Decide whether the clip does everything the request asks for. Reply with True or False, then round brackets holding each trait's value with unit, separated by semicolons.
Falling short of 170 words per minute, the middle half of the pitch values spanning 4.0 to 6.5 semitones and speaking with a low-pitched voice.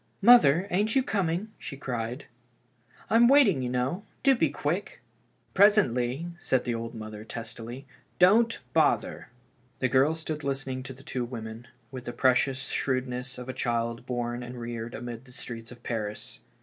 False (175 wpm; 5.1 semitones; 130 Hz)